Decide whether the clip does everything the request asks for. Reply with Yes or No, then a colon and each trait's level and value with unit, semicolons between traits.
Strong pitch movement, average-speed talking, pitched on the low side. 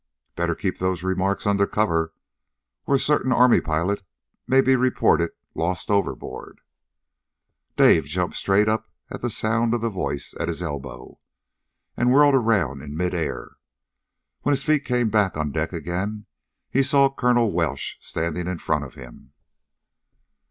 Yes: wide, 6.5 semitones; average, 150 wpm; very low, 95 Hz